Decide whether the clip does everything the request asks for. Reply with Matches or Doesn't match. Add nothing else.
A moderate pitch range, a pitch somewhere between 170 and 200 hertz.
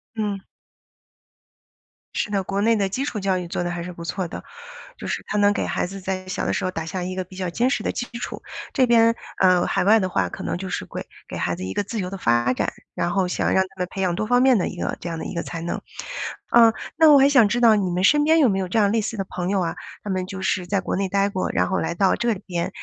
Matches